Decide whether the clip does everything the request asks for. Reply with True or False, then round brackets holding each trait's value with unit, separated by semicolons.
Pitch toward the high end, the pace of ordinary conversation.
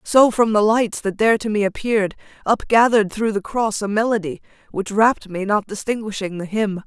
True (210 Hz; 190 wpm)